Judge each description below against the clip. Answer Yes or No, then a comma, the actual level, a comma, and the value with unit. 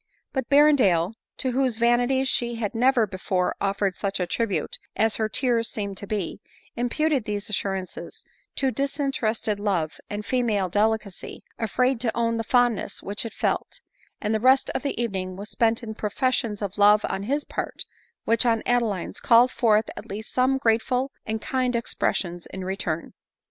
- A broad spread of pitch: No, average, 3.6 semitones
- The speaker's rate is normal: Yes, average, 170 wpm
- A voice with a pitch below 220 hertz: No, high, 225 Hz